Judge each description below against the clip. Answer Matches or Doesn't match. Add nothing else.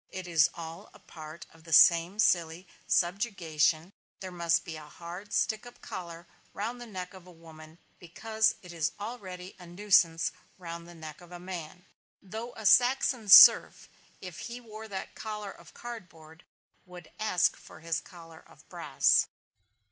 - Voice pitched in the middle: Matches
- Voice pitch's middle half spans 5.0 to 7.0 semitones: Doesn't match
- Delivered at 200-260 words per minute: Doesn't match